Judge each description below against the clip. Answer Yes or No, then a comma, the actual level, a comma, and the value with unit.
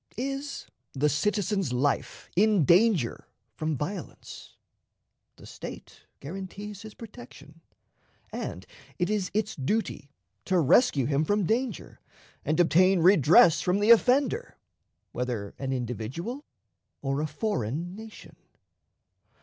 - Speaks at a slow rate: Yes, slow, 110 wpm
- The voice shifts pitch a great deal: Yes, wide, 7.0 semitones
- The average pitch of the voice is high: No, medium, 180 Hz